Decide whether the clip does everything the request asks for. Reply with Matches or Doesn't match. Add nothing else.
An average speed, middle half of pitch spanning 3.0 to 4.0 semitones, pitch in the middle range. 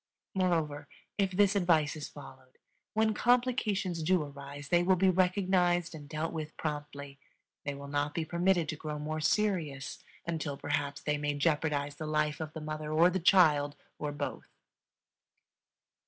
Matches